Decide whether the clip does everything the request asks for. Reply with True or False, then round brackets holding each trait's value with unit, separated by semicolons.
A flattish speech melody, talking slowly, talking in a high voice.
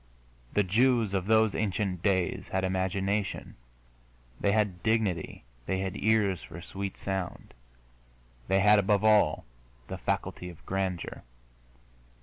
False (2.1 semitones; 125 wpm; 95 Hz)